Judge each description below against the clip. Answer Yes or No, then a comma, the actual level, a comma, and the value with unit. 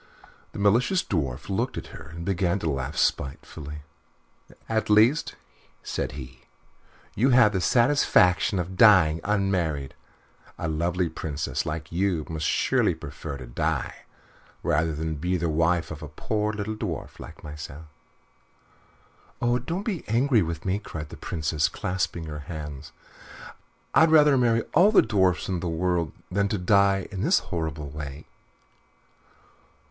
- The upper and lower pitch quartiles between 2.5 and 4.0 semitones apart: No, average, 5.3 semitones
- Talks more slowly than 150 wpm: Yes, average, 140 wpm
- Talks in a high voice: No, very low, 90 Hz